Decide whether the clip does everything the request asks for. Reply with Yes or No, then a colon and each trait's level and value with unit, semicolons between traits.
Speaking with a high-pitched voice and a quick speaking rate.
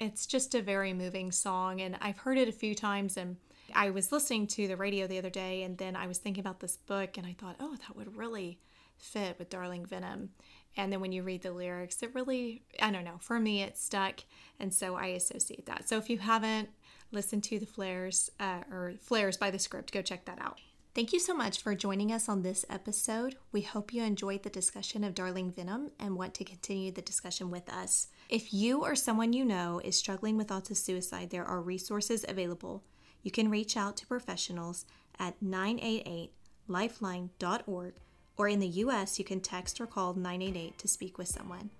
Yes: high, 195 Hz; fast, 210 wpm